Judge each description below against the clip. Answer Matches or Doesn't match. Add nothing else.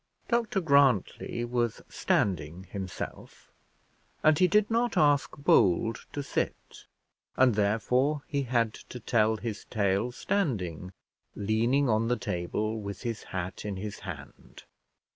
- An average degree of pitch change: Doesn't match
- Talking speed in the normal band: Doesn't match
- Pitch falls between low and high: Doesn't match